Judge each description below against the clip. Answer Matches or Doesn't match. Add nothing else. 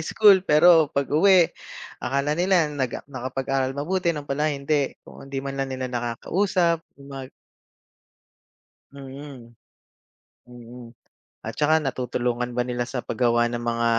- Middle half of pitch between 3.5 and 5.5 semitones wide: Matches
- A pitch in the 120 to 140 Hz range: Matches